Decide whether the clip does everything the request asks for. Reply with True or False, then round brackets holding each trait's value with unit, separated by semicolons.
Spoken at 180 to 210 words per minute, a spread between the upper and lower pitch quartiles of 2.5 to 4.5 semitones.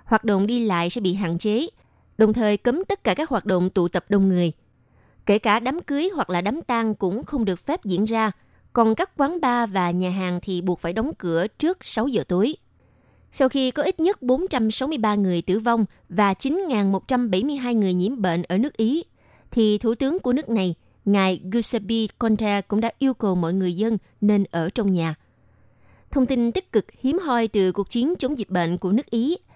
False (205 wpm; 5.3 semitones)